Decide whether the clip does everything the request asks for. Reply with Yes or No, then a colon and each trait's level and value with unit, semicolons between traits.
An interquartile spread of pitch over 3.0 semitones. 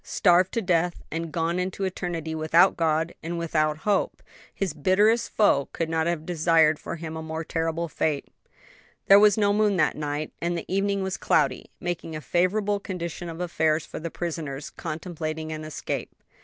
No: average, 2.7 semitones